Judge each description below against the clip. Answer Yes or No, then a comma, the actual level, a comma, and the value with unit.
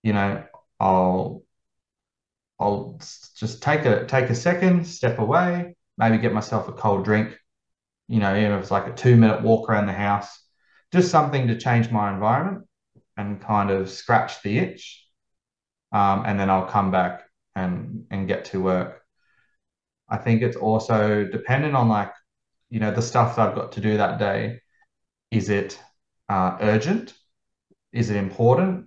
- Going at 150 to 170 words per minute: Yes, average, 165 wpm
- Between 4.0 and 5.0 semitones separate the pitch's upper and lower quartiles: No, average, 3.4 semitones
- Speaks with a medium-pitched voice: No, low, 110 Hz